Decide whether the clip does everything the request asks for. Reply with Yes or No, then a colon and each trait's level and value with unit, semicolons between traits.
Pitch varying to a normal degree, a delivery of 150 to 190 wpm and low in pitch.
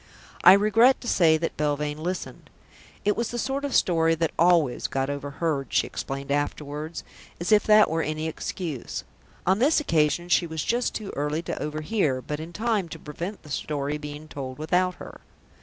No: average, 4.4 semitones; average, 180 wpm; medium, 160 Hz